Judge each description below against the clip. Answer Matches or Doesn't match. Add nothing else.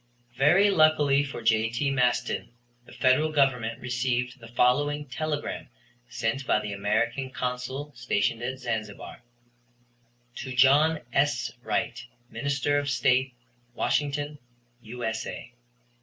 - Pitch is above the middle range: Doesn't match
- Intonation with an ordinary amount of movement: Matches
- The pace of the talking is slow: Matches